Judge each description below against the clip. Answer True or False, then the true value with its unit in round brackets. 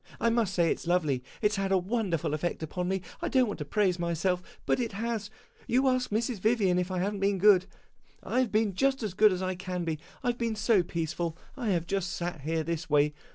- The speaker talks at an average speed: False (245 wpm)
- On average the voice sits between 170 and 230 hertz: True (190 Hz)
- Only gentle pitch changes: False (4.0 semitones)